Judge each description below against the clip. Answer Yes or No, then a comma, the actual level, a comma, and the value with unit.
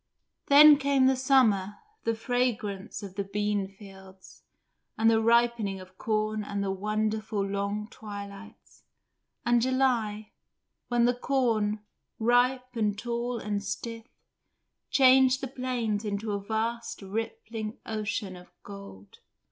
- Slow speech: Yes, slow, 120 wpm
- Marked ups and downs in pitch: No, average, 3.1 semitones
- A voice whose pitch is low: No, high, 220 Hz